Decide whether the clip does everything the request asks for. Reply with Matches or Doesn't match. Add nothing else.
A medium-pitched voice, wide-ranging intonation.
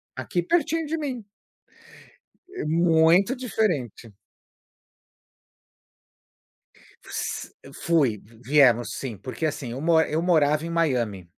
Matches